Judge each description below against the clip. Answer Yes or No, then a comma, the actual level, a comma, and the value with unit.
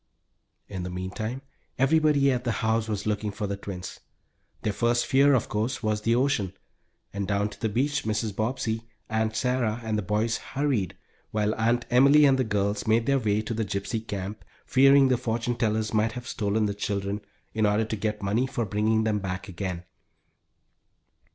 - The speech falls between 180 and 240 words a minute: Yes, average, 185 wpm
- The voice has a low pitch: Yes, low, 110 Hz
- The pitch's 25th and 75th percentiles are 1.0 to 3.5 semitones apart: Yes, average, 2.9 semitones